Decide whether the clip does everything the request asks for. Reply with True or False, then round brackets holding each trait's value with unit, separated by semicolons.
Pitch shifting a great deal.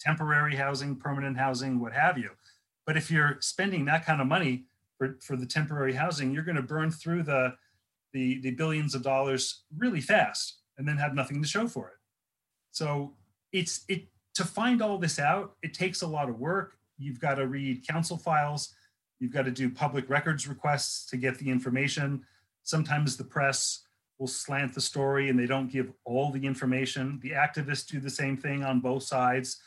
False (2.7 semitones)